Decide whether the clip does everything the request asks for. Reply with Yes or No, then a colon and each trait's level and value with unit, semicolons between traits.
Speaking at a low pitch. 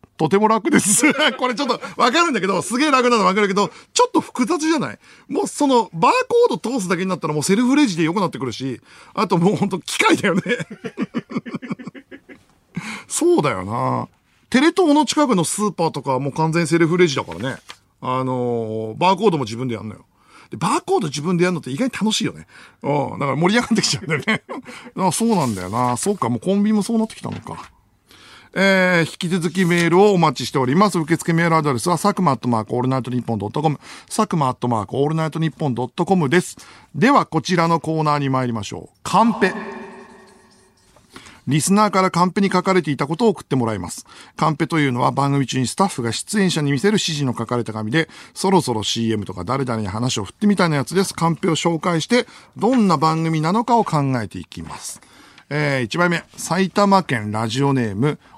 No: medium, 170 Hz